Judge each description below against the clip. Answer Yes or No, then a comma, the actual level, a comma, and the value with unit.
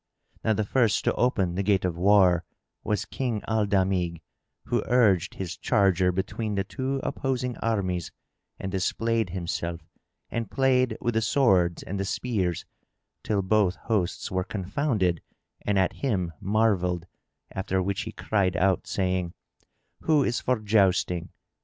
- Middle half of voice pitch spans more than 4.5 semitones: No, average, 3.6 semitones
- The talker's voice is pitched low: Yes, low, 100 Hz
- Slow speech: No, average, 145 wpm